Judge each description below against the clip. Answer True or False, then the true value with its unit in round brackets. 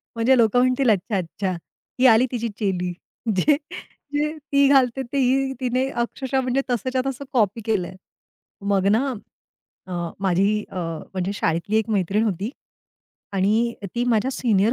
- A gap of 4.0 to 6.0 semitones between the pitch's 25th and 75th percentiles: True (4.5 semitones)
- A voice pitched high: True (230 Hz)